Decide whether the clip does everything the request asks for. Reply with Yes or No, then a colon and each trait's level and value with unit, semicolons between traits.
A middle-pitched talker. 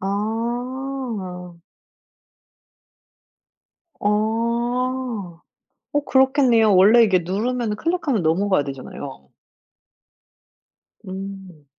No: high, 215 Hz